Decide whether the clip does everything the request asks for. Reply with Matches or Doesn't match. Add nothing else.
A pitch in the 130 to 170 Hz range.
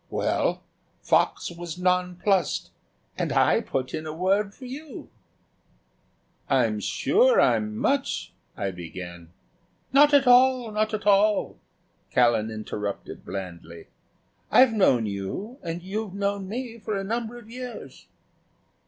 Doesn't match